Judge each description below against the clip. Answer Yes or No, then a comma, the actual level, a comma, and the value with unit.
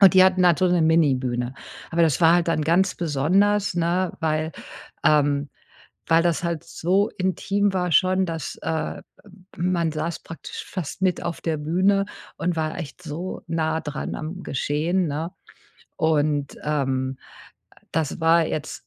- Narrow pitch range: No, average, 3.0 semitones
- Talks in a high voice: No, medium, 165 Hz